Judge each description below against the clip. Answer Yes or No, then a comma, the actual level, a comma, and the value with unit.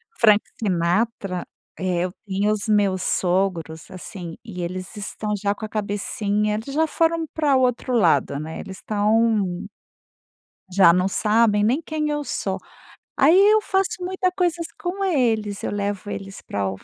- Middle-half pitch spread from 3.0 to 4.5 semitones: No, wide, 5.5 semitones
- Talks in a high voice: Yes, high, 210 Hz